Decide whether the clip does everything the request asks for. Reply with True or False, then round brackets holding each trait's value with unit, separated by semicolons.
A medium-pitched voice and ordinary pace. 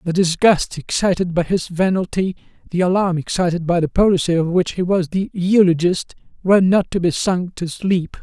True (180 Hz; 180 wpm)